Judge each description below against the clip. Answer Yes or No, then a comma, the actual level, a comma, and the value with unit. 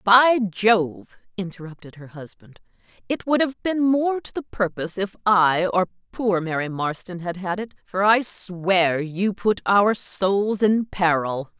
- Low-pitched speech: No, high, 195 Hz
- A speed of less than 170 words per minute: Yes, average, 160 wpm